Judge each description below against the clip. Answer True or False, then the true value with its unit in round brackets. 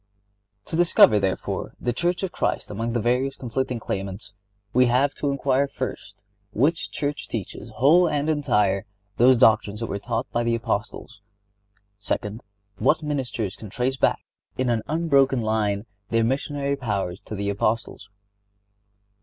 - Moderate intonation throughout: True (4.8 semitones)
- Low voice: True (120 Hz)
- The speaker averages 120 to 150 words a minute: True (145 wpm)